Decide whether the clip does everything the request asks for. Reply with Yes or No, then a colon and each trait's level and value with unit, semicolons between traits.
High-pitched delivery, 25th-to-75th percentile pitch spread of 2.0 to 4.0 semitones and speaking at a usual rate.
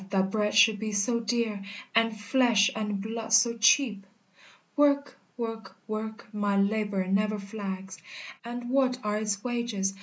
Yes: high, 215 Hz; narrow, 2.4 semitones; average, 145 wpm